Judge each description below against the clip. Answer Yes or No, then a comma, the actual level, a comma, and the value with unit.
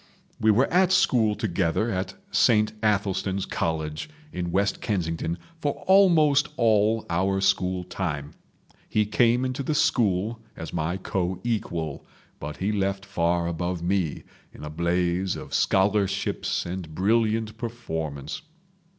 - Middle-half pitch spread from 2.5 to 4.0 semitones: No, average, 4.4 semitones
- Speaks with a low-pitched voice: Yes, very low, 95 Hz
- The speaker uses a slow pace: Yes, slow, 130 wpm